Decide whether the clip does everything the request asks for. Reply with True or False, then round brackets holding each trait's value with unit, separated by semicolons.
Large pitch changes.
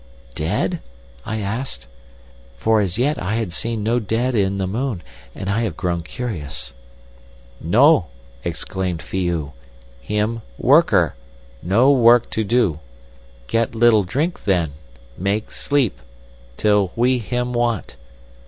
True (5.9 semitones)